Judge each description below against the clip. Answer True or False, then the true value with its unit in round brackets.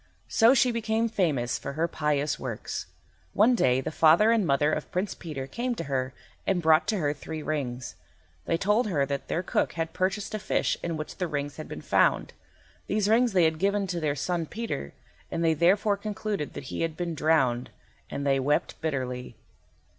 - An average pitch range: False (5.9 semitones)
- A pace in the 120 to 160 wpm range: False (195 wpm)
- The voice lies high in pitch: False (160 Hz)